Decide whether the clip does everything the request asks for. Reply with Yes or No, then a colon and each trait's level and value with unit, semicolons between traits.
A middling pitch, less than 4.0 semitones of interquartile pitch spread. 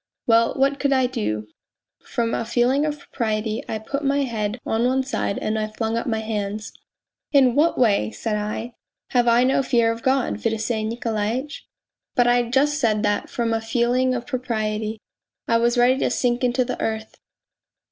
No: high, 235 Hz; average, 2.7 semitones